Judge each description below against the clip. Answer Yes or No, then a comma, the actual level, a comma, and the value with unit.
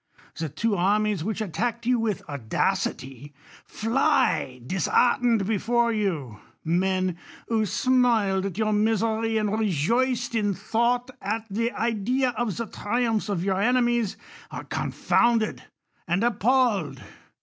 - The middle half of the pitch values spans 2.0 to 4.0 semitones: Yes, average, 3.7 semitones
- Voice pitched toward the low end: No, high, 215 Hz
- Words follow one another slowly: Yes, slow, 130 wpm